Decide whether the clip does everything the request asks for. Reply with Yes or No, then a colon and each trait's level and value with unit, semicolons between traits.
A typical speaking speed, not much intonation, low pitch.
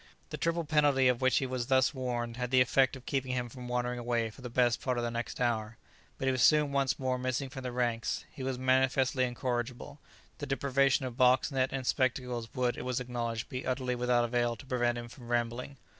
No: fast, 225 wpm; narrow, 1.6 semitones; low, 125 Hz